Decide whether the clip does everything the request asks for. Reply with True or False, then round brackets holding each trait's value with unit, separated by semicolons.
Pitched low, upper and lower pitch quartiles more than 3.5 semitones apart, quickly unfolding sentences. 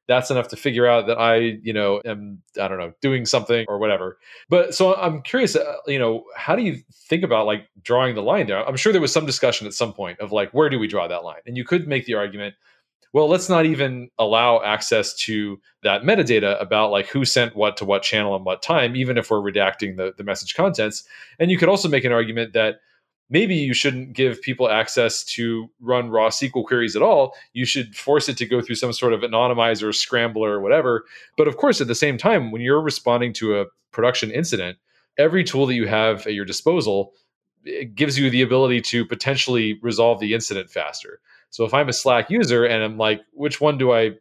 True (120 Hz; 3.9 semitones; 225 wpm)